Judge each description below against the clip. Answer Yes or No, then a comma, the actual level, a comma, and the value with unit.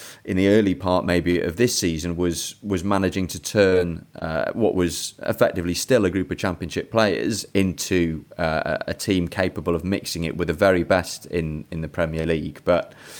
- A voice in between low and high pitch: No, very low, 90 Hz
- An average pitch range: No, narrow, 1.8 semitones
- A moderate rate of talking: Yes, average, 185 wpm